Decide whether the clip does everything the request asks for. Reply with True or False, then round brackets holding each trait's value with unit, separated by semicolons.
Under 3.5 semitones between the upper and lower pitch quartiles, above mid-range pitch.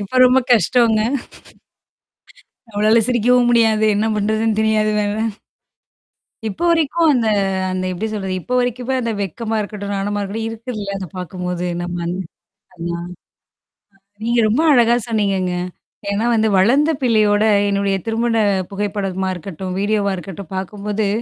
True (2.9 semitones; 210 Hz)